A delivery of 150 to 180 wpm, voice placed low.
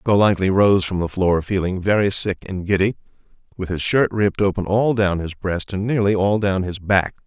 No: fast, 205 wpm; very low, 95 Hz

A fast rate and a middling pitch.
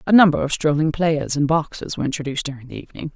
Yes: fast, 230 wpm; medium, 150 Hz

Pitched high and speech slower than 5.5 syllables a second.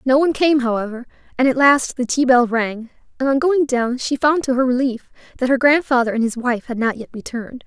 No: very high, 255 Hz; 5.7 syllables/s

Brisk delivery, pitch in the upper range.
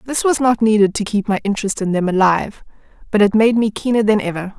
Yes: fast, 235 wpm; high, 210 Hz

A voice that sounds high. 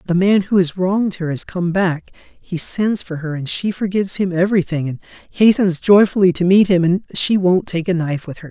No: medium, 180 Hz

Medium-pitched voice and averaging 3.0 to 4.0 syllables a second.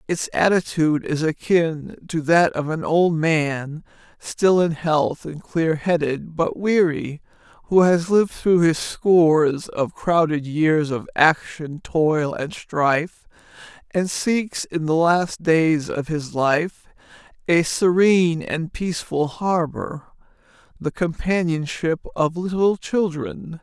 Yes: medium, 165 Hz; 3.6 syllables/s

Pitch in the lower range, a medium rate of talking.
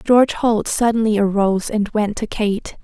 No: high, 215 Hz; average, 170 wpm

